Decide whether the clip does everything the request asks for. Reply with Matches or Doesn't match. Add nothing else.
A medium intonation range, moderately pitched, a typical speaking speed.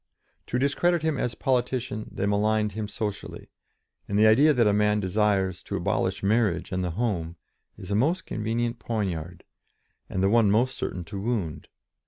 Doesn't match